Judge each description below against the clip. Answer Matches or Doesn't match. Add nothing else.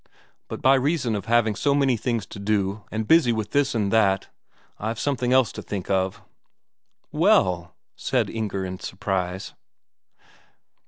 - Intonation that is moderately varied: Matches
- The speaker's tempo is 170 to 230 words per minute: Doesn't match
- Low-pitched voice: Matches